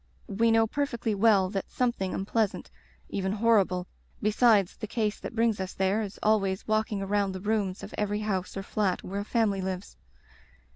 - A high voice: Yes, high, 205 Hz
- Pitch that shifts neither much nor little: No, narrow, 2.3 semitones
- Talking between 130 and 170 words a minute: No, average, 190 wpm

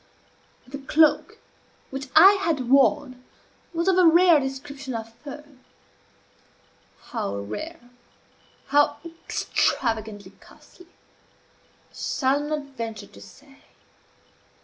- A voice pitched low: No, very high, 275 Hz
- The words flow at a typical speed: No, slow, 100 wpm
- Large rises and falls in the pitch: No, average, 4.7 semitones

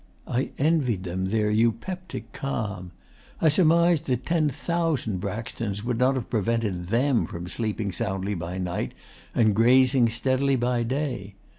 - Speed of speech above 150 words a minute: No, average, 140 wpm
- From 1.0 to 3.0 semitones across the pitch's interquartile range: No, average, 5.0 semitones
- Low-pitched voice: Yes, low, 115 Hz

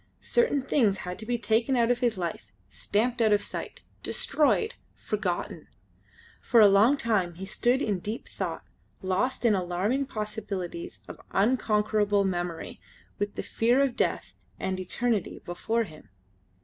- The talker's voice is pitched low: No, high, 215 Hz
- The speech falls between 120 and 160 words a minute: Yes, average, 150 wpm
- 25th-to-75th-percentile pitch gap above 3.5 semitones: Yes, average, 4.2 semitones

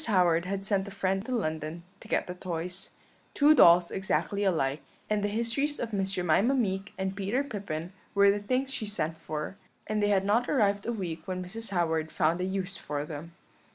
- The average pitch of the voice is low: No, high, 195 Hz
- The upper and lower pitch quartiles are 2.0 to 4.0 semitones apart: Yes, average, 3.5 semitones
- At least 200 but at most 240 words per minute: Yes, fast, 205 wpm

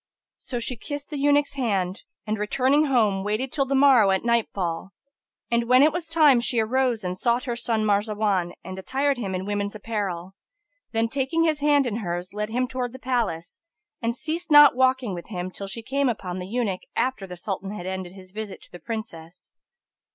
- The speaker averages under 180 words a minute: No, average, 195 wpm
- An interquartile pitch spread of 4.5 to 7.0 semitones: Yes, average, 5.3 semitones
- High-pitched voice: Yes, high, 225 Hz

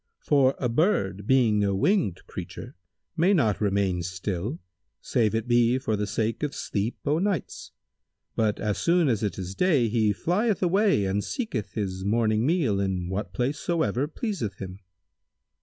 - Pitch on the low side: Yes, low, 115 Hz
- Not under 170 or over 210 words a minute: No, average, 160 wpm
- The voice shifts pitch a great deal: Yes, wide, 7.1 semitones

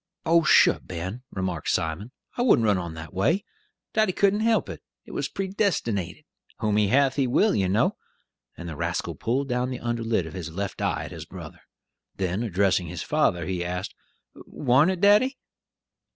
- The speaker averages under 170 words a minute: No, average, 180 wpm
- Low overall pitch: Yes, low, 110 Hz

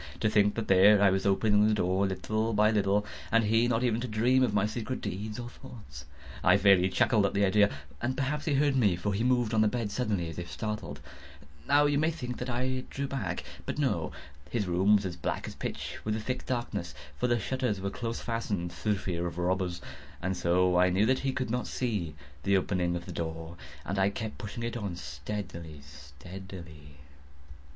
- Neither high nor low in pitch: No, low, 105 Hz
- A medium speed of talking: No, fast, 210 wpm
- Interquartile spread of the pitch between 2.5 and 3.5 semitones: No, average, 4.5 semitones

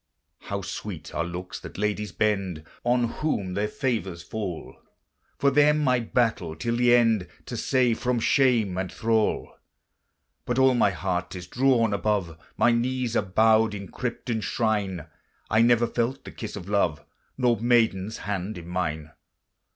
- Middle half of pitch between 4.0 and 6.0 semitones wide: Yes, average, 4.4 semitones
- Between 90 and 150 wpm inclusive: No, average, 160 wpm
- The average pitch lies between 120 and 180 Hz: No, low, 110 Hz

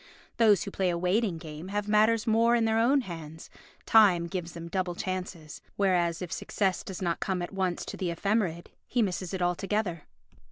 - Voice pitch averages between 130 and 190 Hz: Yes, medium, 185 Hz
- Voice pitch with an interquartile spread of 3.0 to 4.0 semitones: Yes, average, 3.6 semitones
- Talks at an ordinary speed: Yes, average, 190 wpm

